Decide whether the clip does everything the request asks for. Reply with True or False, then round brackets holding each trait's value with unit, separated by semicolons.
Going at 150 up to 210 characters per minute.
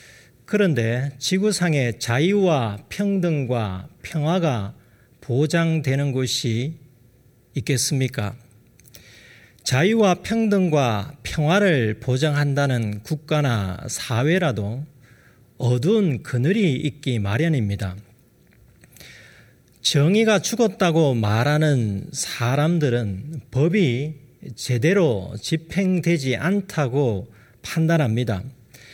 True (190 characters per minute)